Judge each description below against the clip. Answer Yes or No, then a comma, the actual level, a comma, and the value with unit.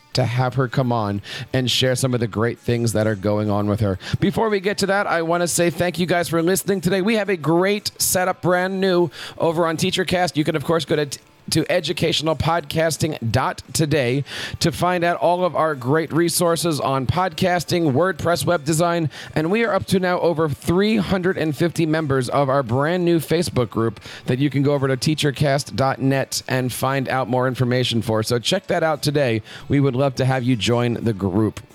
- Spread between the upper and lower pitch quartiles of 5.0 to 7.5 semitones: Yes, average, 5.3 semitones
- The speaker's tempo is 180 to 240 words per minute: Yes, average, 200 wpm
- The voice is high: No, medium, 155 Hz